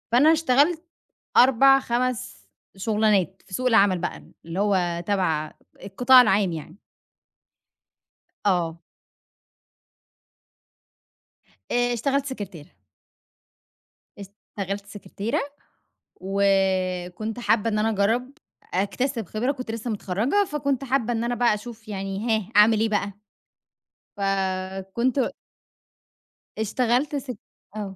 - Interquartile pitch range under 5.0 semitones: Yes, average, 4.2 semitones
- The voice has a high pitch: Yes, high, 215 Hz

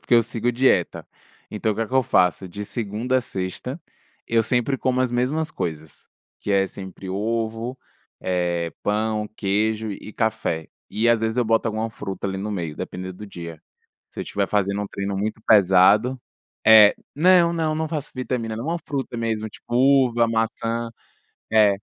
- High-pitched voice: No, low, 110 Hz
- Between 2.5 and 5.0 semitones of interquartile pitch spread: Yes, average, 3.6 semitones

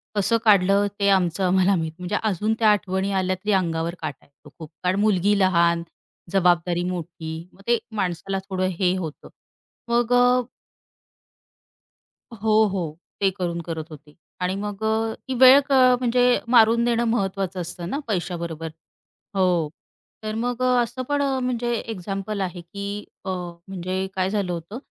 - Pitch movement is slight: No, average, 3.7 semitones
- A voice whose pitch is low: No, high, 190 Hz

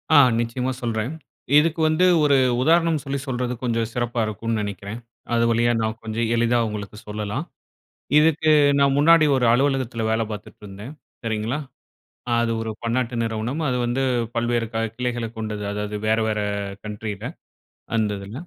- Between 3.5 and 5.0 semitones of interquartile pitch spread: No, average, 3.1 semitones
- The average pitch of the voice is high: No, low, 115 Hz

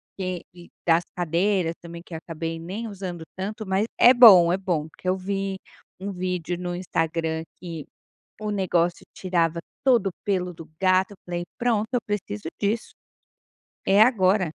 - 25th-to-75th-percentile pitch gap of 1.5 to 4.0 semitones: Yes, average, 2.8 semitones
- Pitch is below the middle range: No, medium, 185 Hz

